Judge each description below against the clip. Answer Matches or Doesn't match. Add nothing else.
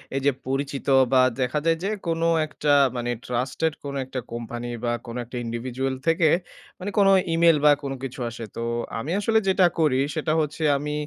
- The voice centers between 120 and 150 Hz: Matches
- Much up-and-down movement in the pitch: Doesn't match